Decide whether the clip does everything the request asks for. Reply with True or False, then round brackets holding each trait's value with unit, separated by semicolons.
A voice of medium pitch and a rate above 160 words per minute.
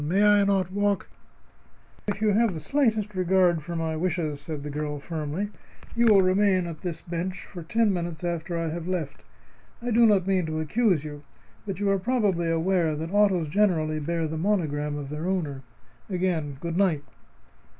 True (175 Hz; 185 wpm)